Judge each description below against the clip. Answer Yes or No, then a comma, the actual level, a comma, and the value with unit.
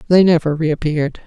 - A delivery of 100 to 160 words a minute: Yes, average, 140 wpm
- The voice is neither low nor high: Yes, medium, 160 Hz